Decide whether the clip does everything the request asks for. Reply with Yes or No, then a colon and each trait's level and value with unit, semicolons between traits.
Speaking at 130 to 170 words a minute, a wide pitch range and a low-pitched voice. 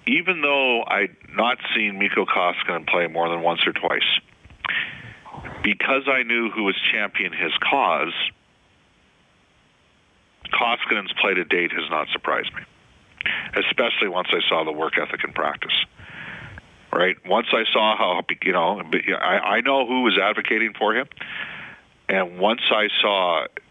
Yes: average, 140 wpm; wide, 7.6 semitones; low, 115 Hz